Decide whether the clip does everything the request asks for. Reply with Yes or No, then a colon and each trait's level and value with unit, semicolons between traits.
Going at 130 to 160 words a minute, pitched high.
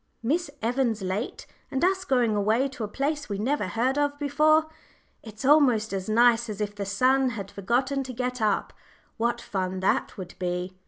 No: average, 180 wpm; high, 235 Hz